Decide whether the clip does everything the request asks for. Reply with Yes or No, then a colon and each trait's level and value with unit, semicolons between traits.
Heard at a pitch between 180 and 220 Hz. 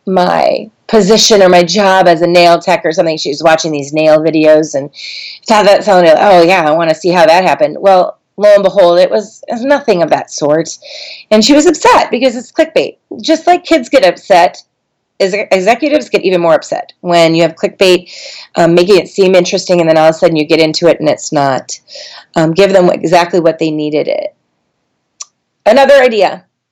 Yes: high, 190 Hz